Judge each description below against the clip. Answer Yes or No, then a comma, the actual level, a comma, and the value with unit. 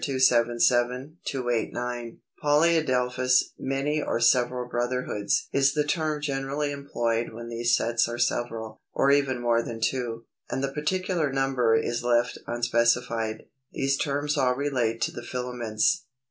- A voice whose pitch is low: Yes, low, 125 Hz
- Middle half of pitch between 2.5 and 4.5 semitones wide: Yes, average, 2.8 semitones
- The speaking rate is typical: No, slow, 130 wpm